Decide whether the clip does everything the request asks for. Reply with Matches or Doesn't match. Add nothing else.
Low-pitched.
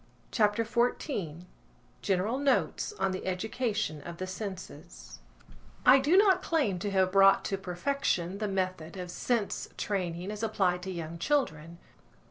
Doesn't match